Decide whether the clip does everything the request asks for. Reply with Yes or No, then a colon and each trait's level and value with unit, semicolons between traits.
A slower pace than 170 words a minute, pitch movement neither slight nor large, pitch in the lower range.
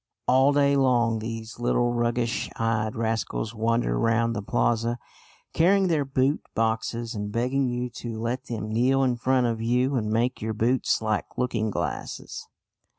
No: average, 155 wpm; narrow, 2.3 semitones; low, 120 Hz